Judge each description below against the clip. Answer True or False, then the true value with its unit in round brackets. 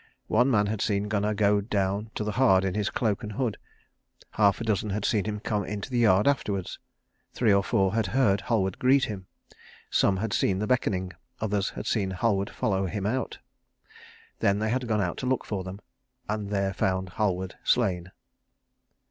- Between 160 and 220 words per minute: True (190 wpm)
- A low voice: True (105 Hz)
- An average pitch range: False (2.2 semitones)